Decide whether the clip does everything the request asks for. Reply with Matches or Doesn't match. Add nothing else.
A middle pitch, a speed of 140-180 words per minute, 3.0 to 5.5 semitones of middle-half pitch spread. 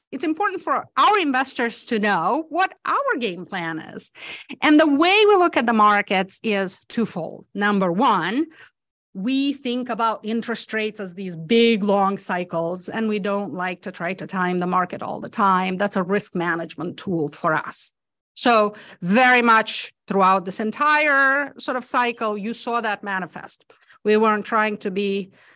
Doesn't match